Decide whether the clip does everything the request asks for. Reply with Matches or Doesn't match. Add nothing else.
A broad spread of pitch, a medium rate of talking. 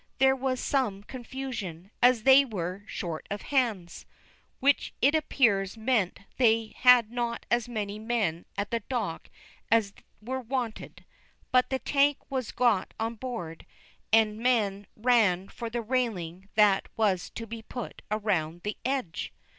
Doesn't match